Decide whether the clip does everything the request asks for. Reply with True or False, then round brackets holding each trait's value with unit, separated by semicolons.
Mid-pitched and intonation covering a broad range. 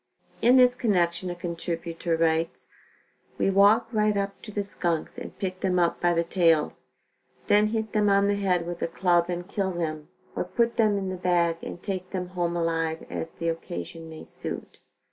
False (180 Hz; 3.1 semitones)